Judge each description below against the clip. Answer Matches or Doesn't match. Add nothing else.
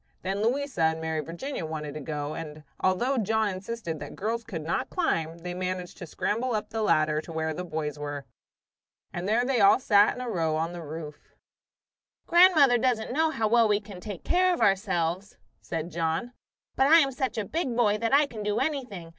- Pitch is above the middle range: Matches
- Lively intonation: Matches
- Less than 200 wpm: Doesn't match